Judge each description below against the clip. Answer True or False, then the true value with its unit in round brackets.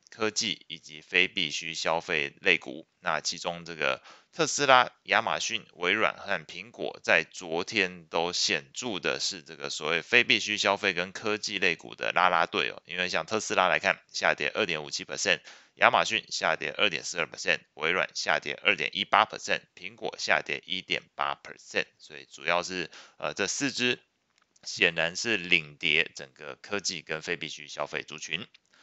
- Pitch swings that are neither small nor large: True (4.7 semitones)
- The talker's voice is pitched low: True (90 Hz)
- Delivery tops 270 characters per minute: True (305 characters per minute)